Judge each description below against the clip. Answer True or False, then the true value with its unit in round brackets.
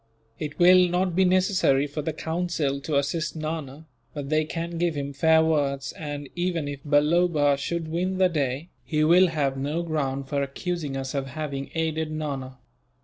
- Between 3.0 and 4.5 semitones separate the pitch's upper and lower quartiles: True (3.3 semitones)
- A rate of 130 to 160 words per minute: False (175 wpm)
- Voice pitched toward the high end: False (155 Hz)